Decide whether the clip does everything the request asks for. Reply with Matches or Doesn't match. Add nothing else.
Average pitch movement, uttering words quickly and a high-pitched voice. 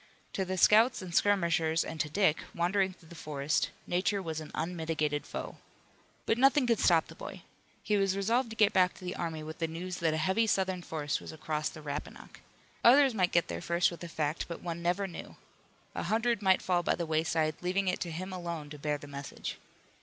Doesn't match